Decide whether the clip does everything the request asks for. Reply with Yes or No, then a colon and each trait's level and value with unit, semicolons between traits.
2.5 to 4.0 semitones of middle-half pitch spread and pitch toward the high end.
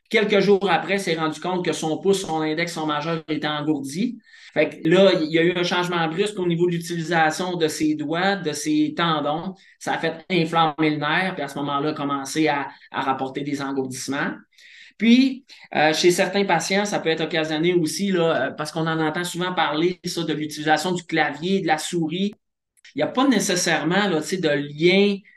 No: average, 3.1 semitones; medium, 165 Hz